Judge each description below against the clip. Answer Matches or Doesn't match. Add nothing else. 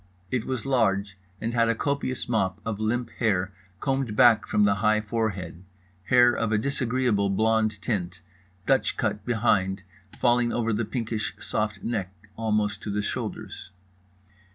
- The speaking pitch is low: Matches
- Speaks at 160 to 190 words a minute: Doesn't match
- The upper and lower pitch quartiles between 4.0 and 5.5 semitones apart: Doesn't match